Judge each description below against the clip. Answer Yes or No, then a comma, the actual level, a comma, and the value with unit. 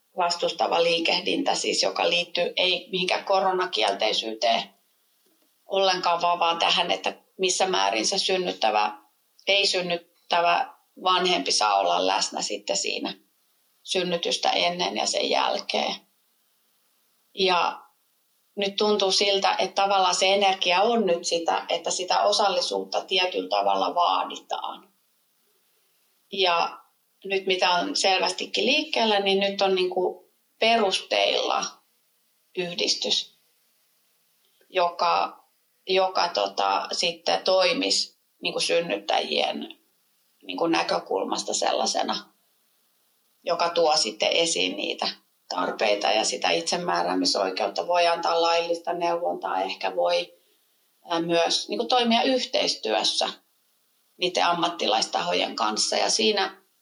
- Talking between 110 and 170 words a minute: No, average, 100 wpm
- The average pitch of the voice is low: No, medium, 175 Hz